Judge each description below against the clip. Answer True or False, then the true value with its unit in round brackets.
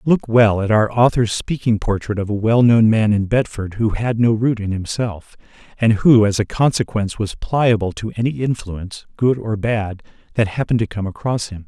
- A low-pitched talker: True (110 Hz)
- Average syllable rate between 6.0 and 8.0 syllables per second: False (5.0 syllables/s)